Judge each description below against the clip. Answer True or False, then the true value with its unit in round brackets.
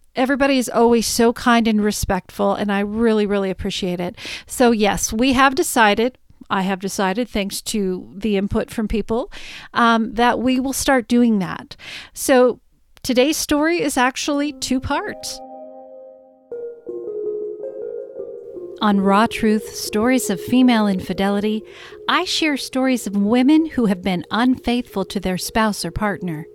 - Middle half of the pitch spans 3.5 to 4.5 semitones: False (4.9 semitones)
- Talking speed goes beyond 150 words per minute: False (140 wpm)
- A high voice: True (230 Hz)